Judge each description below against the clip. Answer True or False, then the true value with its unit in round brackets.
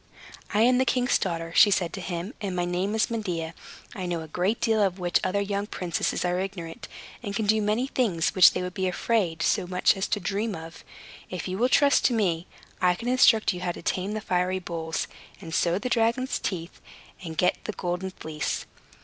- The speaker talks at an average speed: False (215 wpm)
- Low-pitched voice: False (185 Hz)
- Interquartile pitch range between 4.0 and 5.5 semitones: False (3.6 semitones)